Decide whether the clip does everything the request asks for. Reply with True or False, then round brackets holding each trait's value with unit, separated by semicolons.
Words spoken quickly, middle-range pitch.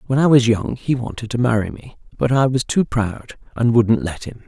False (240 wpm; 120 Hz)